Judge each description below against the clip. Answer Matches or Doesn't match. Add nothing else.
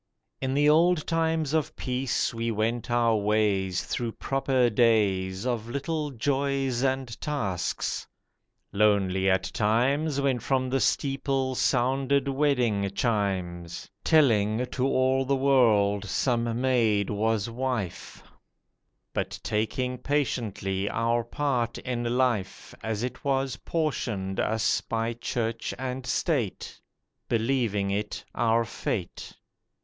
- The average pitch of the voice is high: Doesn't match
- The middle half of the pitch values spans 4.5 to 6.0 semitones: Doesn't match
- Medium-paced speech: Doesn't match